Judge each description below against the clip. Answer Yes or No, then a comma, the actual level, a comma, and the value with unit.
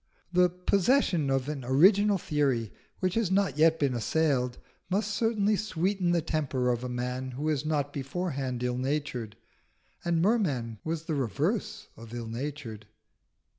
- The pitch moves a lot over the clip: Yes, wide, 6.2 semitones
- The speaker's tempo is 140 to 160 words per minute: Yes, average, 150 wpm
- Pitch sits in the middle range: Yes, medium, 150 Hz